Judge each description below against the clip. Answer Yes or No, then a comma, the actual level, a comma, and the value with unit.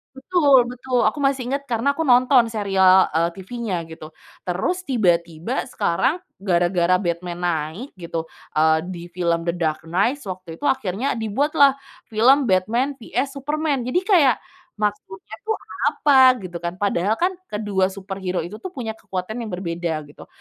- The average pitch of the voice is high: Yes, high, 205 Hz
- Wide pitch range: Yes, wide, 6.9 semitones